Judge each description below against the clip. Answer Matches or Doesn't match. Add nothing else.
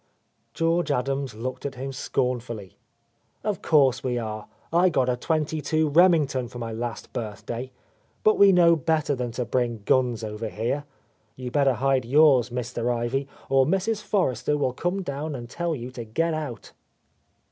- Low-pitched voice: Matches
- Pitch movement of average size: Matches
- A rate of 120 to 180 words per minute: Matches